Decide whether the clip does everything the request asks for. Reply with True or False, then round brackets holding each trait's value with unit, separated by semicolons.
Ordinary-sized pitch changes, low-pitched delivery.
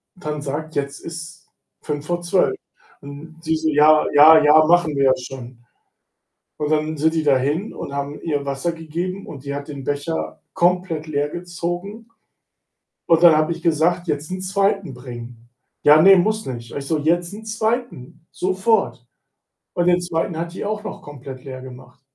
False (3.6 semitones; 155 Hz)